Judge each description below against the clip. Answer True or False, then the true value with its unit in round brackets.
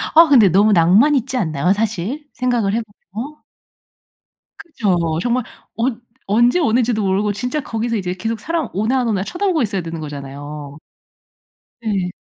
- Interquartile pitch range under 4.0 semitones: False (5.4 semitones)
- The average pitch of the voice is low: False (220 Hz)